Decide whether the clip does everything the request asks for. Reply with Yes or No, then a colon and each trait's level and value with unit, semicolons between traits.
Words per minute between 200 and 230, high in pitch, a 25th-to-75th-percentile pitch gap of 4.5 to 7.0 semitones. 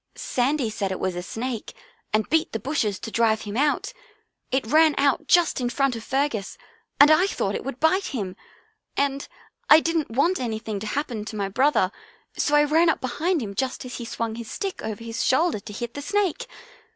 Yes: fast, 205 wpm; very high, 255 Hz; wide, 5.4 semitones